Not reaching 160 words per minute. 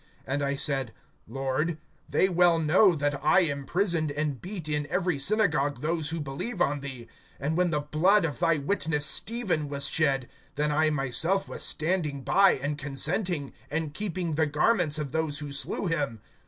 No: average, 170 wpm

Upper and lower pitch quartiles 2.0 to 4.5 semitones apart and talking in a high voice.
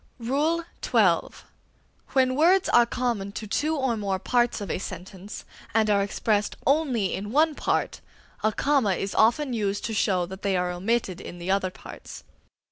No: average, 5.1 semitones; high, 220 Hz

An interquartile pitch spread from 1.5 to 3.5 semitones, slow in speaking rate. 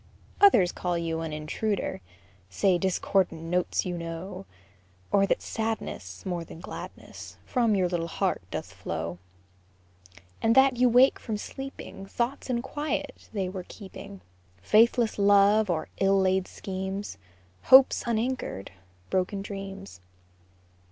No: average, 4.1 semitones; slow, 125 wpm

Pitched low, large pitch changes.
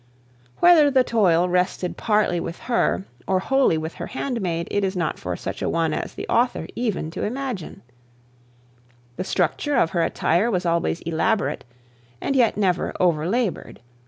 No: medium, 185 Hz; wide, 6.0 semitones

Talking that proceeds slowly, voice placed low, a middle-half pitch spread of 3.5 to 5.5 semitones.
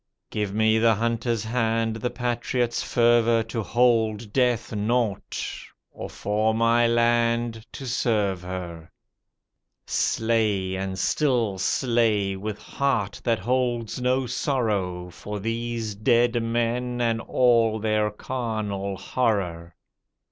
No: slow, 110 wpm; low, 115 Hz; narrow, 2.4 semitones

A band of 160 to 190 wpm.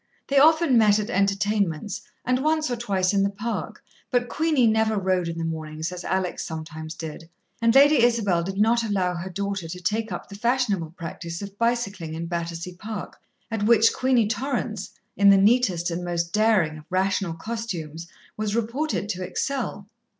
Yes: average, 175 wpm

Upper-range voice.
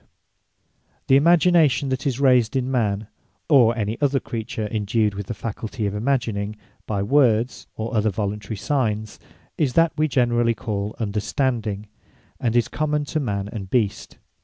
No: low, 115 Hz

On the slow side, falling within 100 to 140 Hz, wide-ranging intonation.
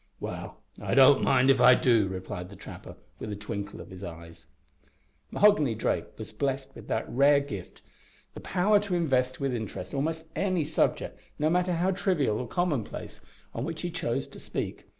No: average, 180 wpm; low, 135 Hz; wide, 7.2 semitones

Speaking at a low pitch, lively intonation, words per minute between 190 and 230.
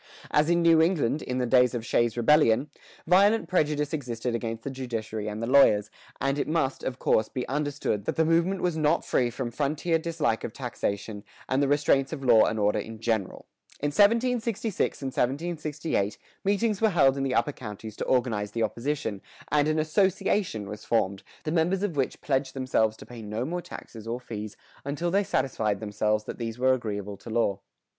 Yes: low, 130 Hz; wide, 5.8 semitones; average, 195 wpm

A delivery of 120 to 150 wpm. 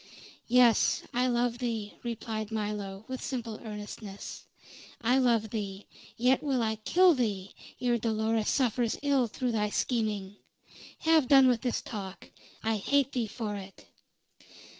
Yes: average, 140 wpm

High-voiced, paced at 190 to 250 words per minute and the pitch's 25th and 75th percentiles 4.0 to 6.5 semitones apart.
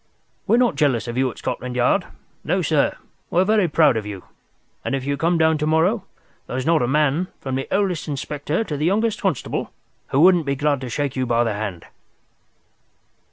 No: medium, 145 Hz; fast, 205 wpm; average, 5.0 semitones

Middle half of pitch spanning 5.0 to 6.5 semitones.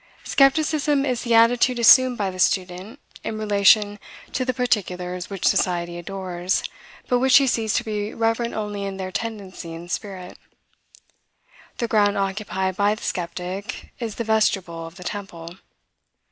No: average, 4.0 semitones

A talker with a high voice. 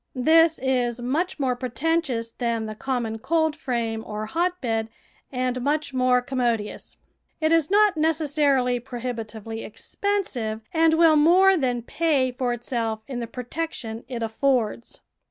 Yes: very high, 255 Hz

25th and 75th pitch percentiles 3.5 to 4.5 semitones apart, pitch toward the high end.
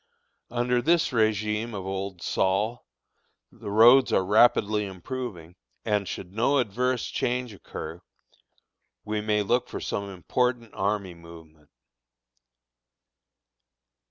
No: average, 4.0 semitones; low, 105 Hz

